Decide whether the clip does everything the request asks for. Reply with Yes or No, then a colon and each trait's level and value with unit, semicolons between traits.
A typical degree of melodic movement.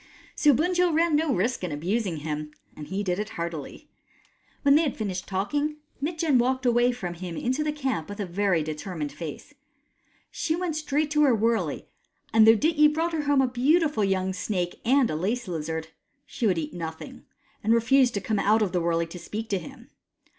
No: wide, 8.4 semitones